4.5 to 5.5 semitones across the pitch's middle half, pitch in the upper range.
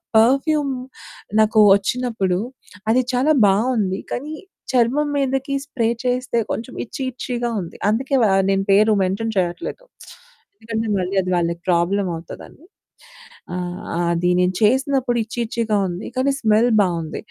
Yes: average, 5.0 semitones; high, 225 Hz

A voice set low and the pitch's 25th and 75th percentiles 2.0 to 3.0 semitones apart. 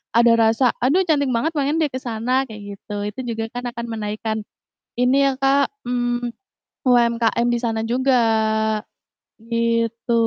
No: high, 240 Hz; narrow, 2.4 semitones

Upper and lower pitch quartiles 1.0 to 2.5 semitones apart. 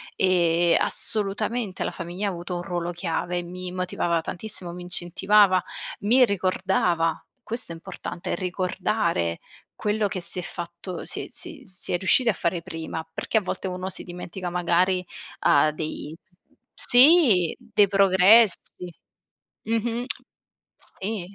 No: average, 2.9 semitones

